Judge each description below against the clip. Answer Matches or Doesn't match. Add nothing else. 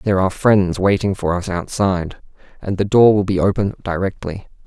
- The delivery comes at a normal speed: Matches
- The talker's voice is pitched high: Doesn't match